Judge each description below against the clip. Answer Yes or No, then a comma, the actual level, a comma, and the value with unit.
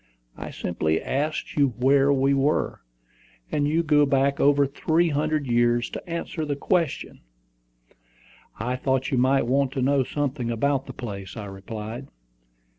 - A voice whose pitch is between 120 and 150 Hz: Yes, low, 135 Hz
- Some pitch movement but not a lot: Yes, average, 3.1 semitones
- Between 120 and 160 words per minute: Yes, average, 150 wpm